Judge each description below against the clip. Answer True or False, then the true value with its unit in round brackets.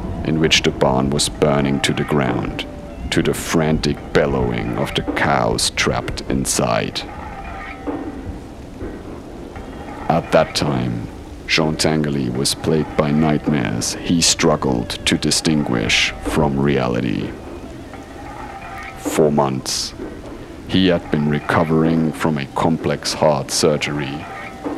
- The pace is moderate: False (105 wpm)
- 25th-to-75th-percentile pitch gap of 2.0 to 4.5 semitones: True (2.7 semitones)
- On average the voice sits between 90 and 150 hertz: False (75 Hz)